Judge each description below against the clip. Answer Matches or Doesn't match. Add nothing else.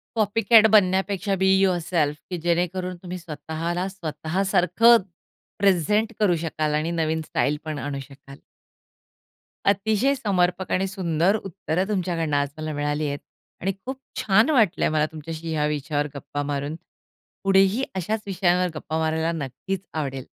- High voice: Doesn't match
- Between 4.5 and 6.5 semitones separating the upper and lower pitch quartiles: Doesn't match